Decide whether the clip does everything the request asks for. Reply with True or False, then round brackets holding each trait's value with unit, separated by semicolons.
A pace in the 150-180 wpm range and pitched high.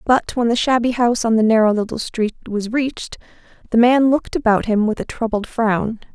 False (205 wpm; 230 Hz)